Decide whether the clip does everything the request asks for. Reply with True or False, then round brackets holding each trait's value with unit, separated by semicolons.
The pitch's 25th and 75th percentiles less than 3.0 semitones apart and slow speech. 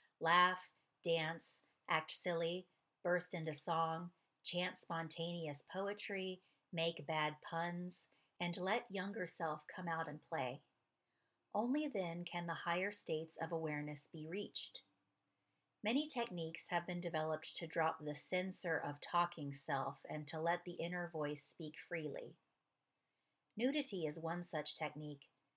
True (2.4 semitones; 130 wpm)